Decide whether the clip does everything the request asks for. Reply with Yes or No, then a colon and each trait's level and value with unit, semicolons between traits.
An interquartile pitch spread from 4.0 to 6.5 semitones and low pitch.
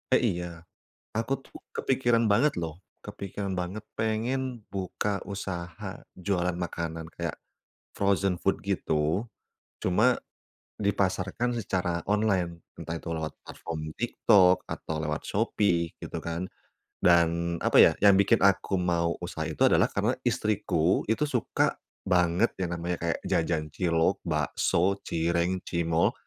No: average, 3.0 semitones; very low, 90 Hz